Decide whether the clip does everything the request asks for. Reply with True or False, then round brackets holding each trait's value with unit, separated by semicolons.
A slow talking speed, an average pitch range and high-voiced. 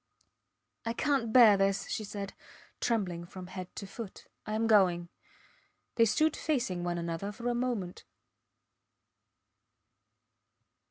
True (120 wpm; 4.2 semitones; 205 Hz)